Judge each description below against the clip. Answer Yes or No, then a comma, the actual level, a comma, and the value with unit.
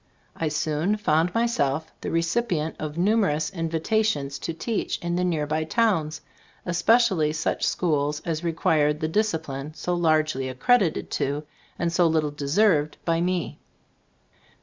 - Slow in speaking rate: Yes, slow, 130 wpm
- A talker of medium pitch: Yes, medium, 160 Hz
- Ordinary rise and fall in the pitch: Yes, average, 3.0 semitones